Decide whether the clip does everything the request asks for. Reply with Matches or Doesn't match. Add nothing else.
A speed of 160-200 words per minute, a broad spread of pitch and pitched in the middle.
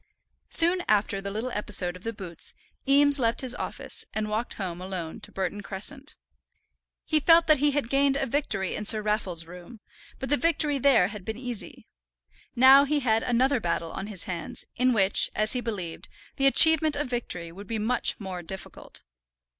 Doesn't match